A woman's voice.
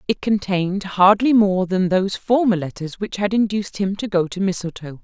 Yes: female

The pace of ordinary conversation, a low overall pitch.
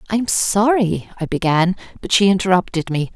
No: average, 170 wpm; high, 190 Hz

